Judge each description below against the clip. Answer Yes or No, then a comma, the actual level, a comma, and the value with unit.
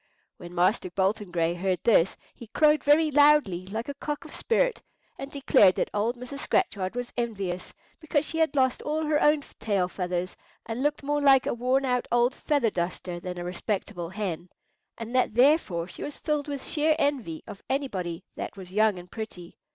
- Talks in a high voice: Yes, high, 230 Hz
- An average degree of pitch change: No, wide, 7.7 semitones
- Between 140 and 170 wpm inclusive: No, average, 190 wpm